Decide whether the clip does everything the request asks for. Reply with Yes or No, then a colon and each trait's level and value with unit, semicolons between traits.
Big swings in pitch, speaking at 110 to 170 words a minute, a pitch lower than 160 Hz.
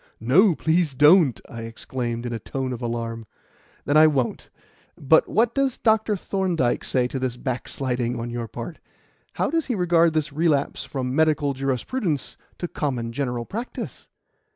Yes: wide, 5.7 semitones; average, 155 wpm; medium, 140 Hz